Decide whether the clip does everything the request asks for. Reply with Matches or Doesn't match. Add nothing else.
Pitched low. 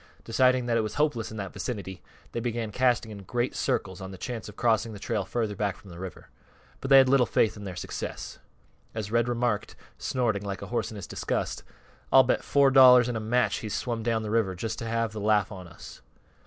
Matches